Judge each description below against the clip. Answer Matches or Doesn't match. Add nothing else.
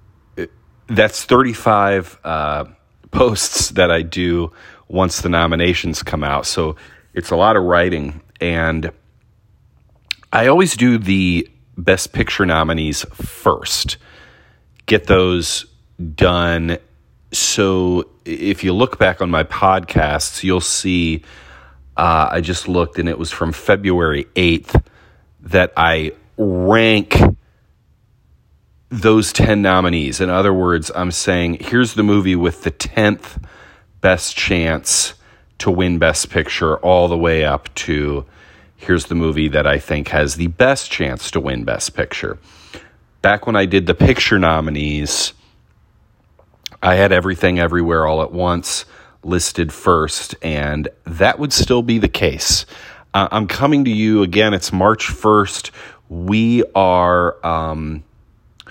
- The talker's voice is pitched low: Matches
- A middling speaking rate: Doesn't match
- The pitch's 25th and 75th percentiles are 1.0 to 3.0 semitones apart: Doesn't match